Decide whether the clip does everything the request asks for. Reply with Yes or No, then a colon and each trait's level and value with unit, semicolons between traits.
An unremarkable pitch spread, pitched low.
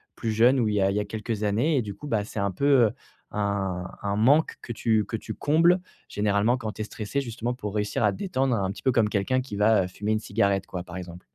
Yes: average, 3.1 semitones; low, 105 Hz